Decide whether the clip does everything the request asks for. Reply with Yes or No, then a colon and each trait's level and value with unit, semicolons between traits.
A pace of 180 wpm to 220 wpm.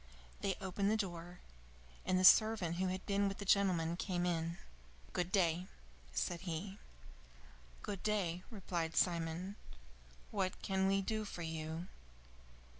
No: slow, 135 wpm